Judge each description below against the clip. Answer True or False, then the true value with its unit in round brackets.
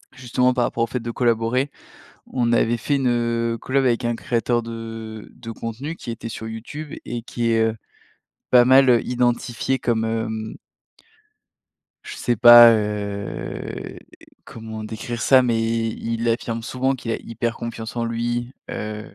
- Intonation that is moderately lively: False (1.4 semitones)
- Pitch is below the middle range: True (115 Hz)